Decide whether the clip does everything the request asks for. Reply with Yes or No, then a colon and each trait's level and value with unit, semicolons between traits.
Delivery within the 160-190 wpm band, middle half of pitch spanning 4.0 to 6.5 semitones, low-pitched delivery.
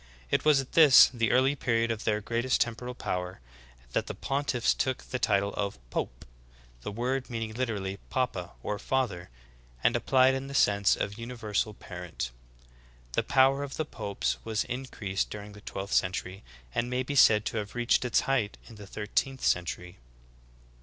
Yes: average, 170 wpm; average, 4.3 semitones; low, 115 Hz